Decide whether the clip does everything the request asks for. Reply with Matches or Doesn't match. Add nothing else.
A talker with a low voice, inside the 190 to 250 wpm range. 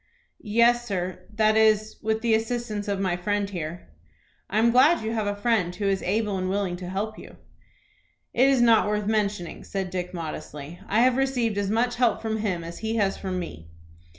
Doesn't match